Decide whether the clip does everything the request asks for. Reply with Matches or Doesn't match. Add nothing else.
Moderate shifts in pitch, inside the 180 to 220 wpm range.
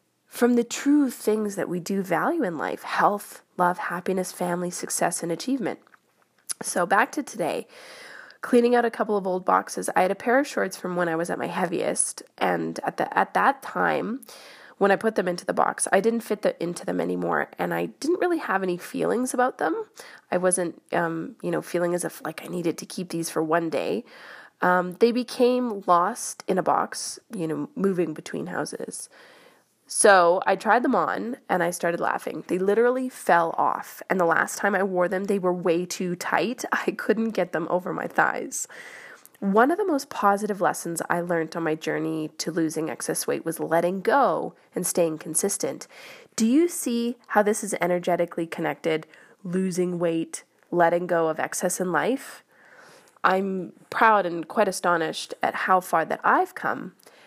Matches